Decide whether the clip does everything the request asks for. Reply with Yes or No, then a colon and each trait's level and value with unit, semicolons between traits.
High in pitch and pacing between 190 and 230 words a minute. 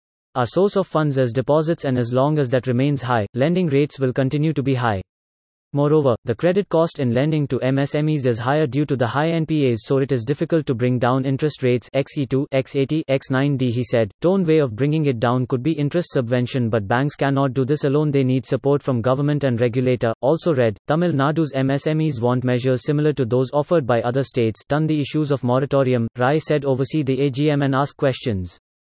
No: low, 135 Hz; fast, 205 wpm